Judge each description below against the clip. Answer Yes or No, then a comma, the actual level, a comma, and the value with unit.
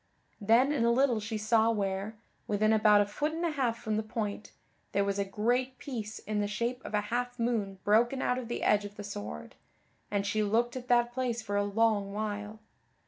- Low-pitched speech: No, high, 220 Hz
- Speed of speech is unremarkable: No, fast, 215 wpm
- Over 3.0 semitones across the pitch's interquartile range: No, average, 2.7 semitones